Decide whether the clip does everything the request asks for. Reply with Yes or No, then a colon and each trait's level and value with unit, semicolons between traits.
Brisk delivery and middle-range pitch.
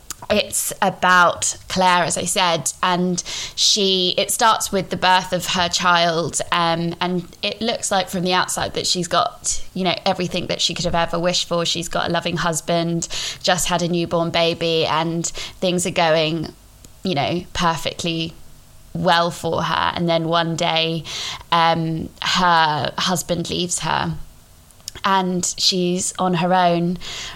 No: average, 155 wpm; medium, 175 Hz